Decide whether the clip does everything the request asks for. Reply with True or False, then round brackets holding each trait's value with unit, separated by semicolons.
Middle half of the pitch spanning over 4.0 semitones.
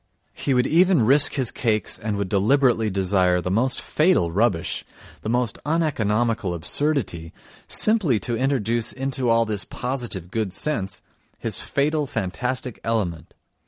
True (5.2 semitones)